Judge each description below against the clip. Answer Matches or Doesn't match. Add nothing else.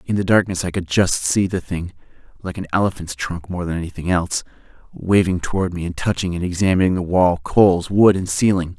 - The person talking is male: Matches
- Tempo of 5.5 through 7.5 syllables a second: Matches